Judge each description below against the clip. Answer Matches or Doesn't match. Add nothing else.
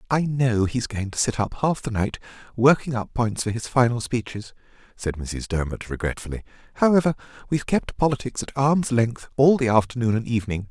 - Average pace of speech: Matches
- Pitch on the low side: Matches